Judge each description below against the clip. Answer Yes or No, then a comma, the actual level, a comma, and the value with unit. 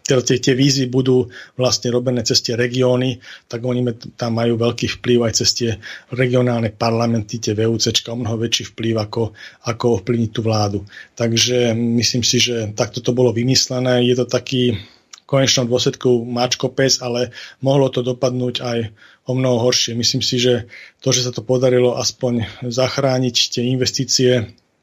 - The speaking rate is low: No, average, 160 wpm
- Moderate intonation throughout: No, narrow, 1.5 semitones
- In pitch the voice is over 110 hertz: Yes, low, 125 Hz